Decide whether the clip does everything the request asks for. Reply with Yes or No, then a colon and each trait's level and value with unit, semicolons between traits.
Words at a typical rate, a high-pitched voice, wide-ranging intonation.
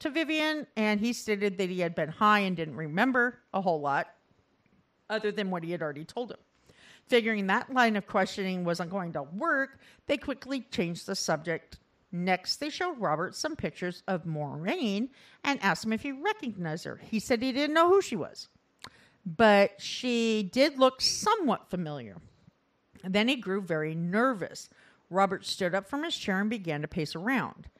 Yes: average, 180 wpm; high, 205 Hz; wide, 6.1 semitones